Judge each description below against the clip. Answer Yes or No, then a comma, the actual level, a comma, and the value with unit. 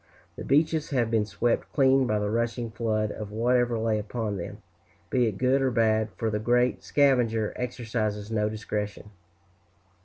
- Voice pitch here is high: No, low, 115 Hz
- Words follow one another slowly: No, average, 160 wpm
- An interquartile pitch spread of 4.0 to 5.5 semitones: No, narrow, 2.5 semitones